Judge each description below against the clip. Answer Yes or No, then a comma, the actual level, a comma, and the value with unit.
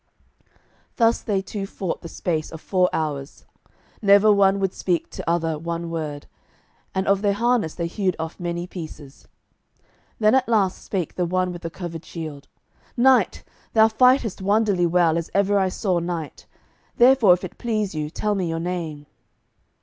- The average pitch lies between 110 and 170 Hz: No, medium, 180 Hz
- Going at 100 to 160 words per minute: No, average, 170 wpm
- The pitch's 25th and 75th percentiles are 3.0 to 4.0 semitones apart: Yes, average, 3.6 semitones